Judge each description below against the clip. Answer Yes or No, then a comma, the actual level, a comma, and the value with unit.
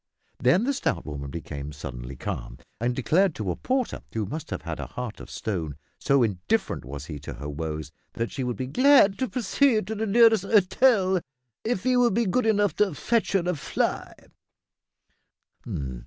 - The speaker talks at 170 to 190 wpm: Yes, average, 185 wpm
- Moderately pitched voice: Yes, medium, 155 Hz